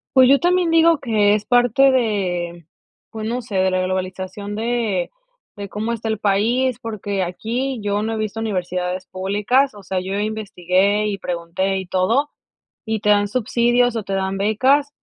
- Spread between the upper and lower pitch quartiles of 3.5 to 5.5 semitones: Yes, average, 4.1 semitones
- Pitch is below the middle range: No, high, 210 Hz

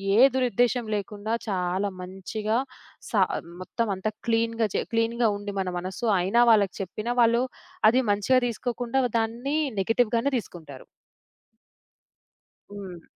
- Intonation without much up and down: No, average, 3.4 semitones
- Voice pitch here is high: Yes, high, 220 Hz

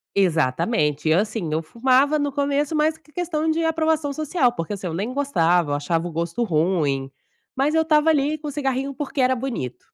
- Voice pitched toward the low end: No, very high, 260 Hz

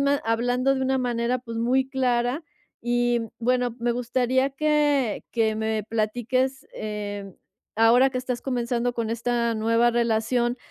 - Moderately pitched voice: No, high, 240 Hz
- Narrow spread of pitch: Yes, narrow, 1.9 semitones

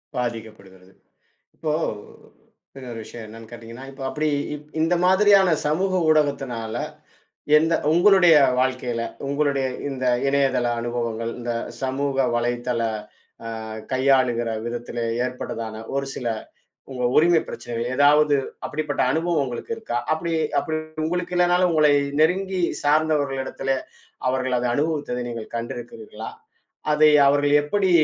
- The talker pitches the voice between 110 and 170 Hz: Yes, low, 135 Hz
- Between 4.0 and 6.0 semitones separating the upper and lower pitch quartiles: Yes, average, 4.6 semitones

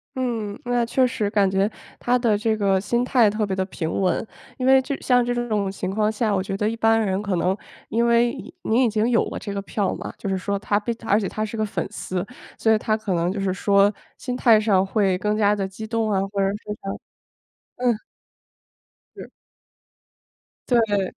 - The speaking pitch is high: Yes, high, 210 Hz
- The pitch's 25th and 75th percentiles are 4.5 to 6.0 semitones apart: No, average, 2.7 semitones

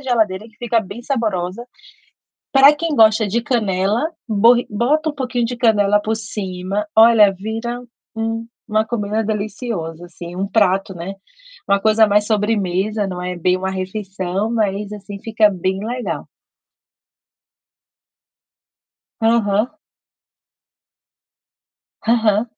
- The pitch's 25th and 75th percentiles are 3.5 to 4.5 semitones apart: No, average, 3.0 semitones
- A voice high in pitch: Yes, high, 215 Hz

